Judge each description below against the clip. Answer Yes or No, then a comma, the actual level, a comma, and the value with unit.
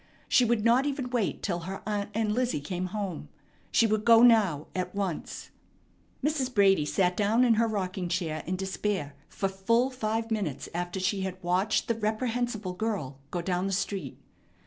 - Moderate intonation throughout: Yes, average, 3.8 semitones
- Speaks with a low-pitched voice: No, high, 200 Hz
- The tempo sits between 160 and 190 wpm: Yes, average, 175 wpm